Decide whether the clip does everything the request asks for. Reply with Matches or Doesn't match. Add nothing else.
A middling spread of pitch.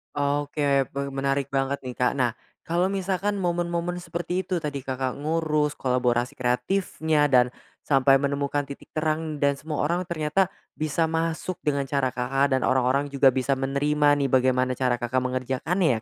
Matches